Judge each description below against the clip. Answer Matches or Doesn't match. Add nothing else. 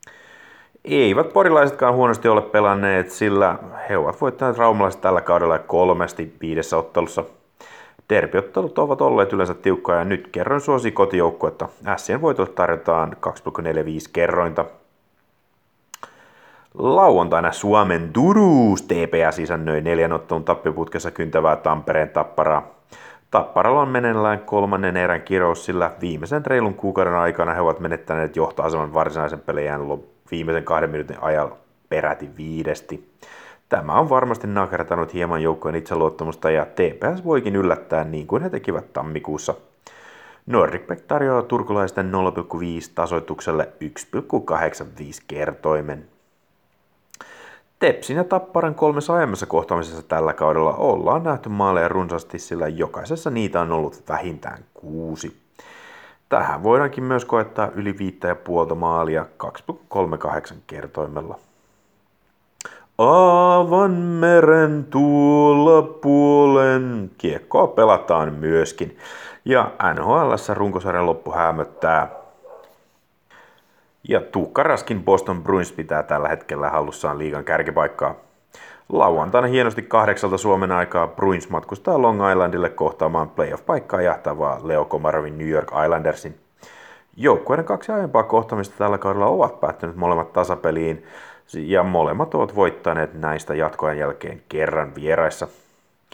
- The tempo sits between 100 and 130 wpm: Matches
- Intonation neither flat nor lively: Doesn't match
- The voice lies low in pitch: Matches